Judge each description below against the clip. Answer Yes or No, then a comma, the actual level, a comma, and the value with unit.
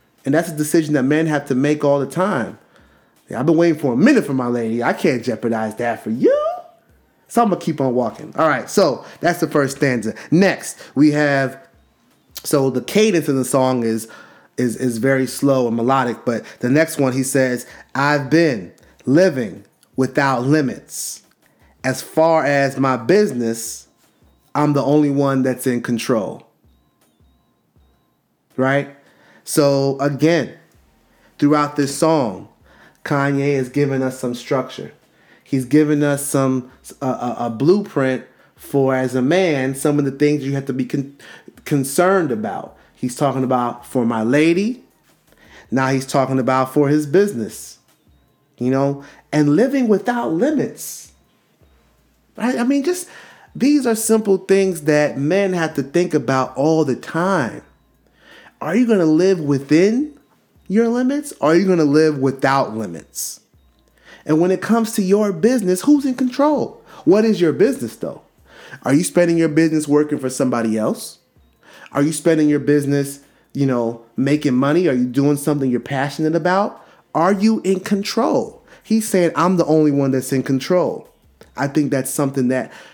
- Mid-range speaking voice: Yes, medium, 145 Hz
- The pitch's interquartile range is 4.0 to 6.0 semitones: Yes, average, 4.3 semitones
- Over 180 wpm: No, average, 165 wpm